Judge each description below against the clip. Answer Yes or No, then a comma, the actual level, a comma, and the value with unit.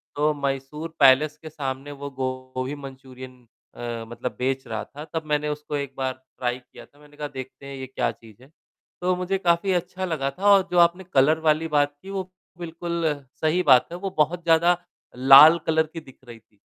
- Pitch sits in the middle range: Yes, medium, 150 Hz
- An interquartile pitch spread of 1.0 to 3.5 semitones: No, average, 4.1 semitones